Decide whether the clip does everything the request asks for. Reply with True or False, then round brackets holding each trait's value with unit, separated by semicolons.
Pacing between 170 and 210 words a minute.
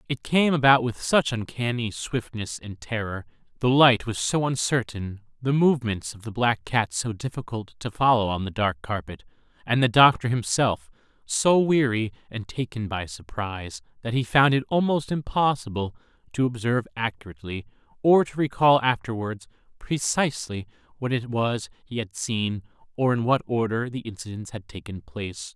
False (155 wpm)